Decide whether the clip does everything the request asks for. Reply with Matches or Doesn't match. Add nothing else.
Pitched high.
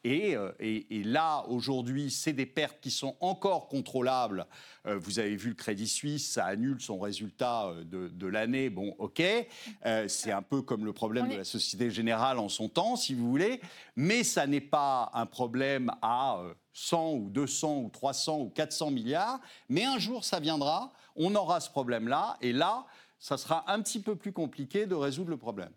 Doesn't match